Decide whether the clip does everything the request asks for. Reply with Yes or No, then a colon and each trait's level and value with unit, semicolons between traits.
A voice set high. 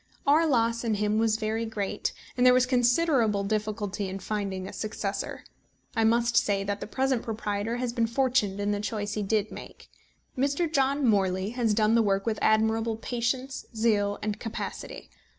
Yes: high, 220 Hz